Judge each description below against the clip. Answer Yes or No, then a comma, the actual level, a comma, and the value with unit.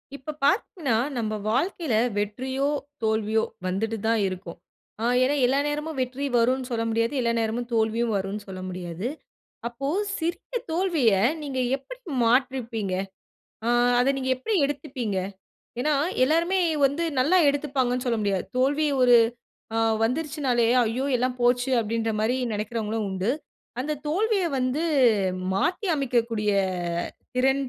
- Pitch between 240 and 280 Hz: Yes, very high, 250 Hz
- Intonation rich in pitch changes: No, average, 4.1 semitones